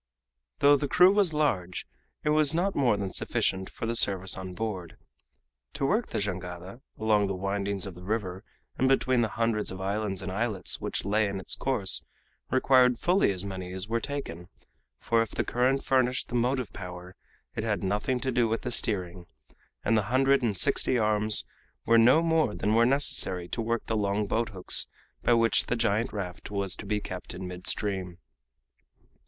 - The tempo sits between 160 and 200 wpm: Yes, average, 185 wpm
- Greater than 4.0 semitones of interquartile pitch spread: Yes, average, 4.7 semitones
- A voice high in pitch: No, low, 110 Hz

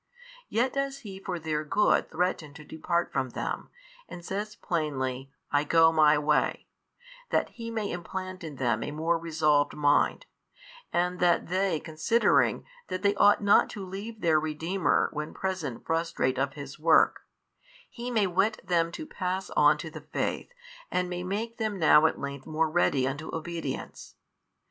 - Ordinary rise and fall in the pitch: Yes, average, 4.2 semitones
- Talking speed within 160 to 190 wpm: Yes, average, 165 wpm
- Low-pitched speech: No, medium, 170 Hz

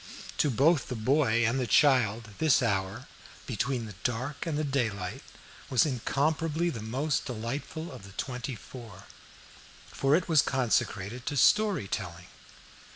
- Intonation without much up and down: No, average, 4.8 semitones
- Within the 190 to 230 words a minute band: No, average, 145 wpm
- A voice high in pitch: No, low, 130 Hz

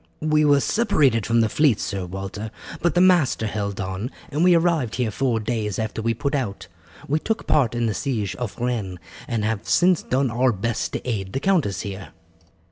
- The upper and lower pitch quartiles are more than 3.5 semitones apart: Yes, wide, 5.6 semitones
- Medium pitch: No, low, 115 Hz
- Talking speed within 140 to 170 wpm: No, average, 200 wpm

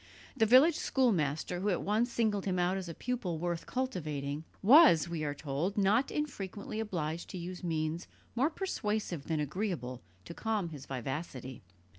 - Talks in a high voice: No, medium, 180 Hz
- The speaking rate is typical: Yes, average, 160 wpm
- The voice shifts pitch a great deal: Yes, wide, 6.0 semitones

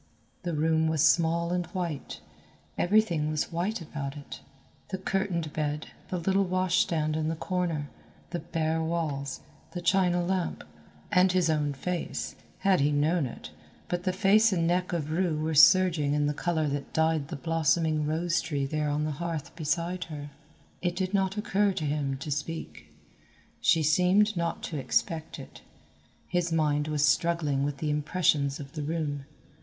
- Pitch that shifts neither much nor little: Yes, average, 3.0 semitones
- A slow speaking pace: No, average, 170 wpm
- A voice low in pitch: No, medium, 160 Hz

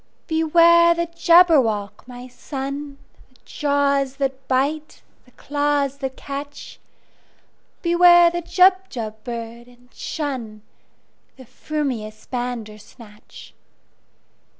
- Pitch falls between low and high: No, very high, 275 Hz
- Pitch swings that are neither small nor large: Yes, average, 4.5 semitones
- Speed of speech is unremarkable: No, slow, 80 wpm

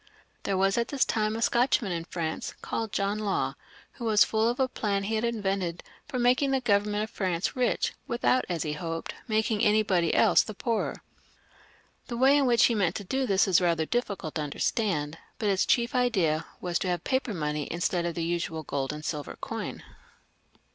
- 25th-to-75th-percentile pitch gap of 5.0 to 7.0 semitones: Yes, wide, 5.5 semitones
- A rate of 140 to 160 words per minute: No, average, 195 wpm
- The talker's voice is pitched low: No, high, 200 Hz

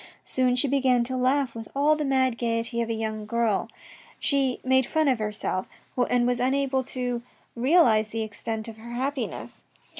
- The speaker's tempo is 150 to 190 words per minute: Yes, average, 175 wpm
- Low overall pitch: No, high, 245 Hz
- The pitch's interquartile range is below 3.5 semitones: Yes, narrow, 2.6 semitones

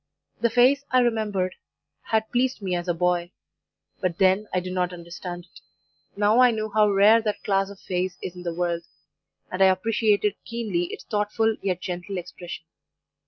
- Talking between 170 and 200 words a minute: Yes, average, 175 wpm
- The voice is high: Yes, high, 195 Hz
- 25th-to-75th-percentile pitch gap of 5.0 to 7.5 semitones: No, average, 3.4 semitones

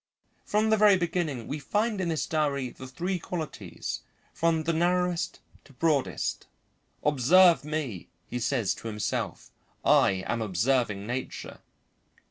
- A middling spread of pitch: No, wide, 6.2 semitones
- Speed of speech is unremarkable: No, slow, 130 wpm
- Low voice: No, medium, 150 Hz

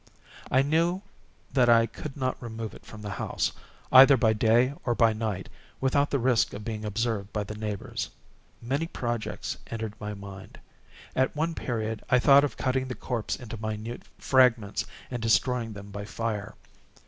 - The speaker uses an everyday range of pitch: Yes, average, 3.3 semitones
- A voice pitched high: No, low, 115 Hz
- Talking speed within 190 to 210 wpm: No, average, 170 wpm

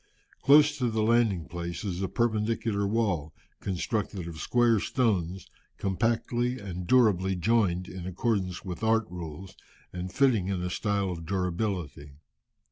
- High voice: No, low, 100 Hz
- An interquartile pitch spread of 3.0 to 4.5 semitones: Yes, average, 4.1 semitones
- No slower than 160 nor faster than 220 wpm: No, slow, 135 wpm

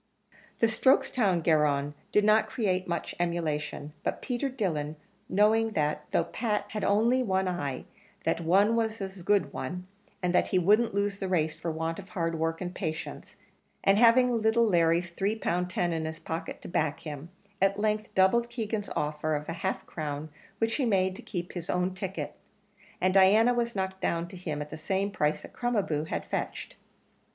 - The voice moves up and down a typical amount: Yes, average, 4.7 semitones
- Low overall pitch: No, medium, 185 Hz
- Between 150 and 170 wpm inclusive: No, average, 190 wpm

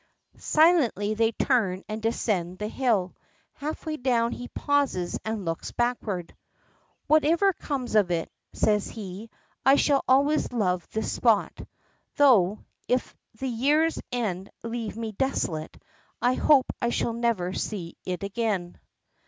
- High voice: Yes, high, 230 Hz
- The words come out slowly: Yes, slow, 130 wpm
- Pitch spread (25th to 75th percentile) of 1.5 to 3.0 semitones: No, average, 5.2 semitones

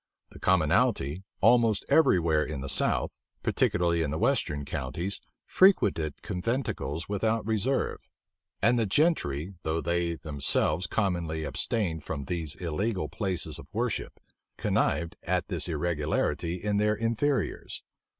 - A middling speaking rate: No, slow, 125 wpm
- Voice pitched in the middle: No, very low, 85 Hz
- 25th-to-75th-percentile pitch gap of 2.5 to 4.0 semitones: No, average, 5.2 semitones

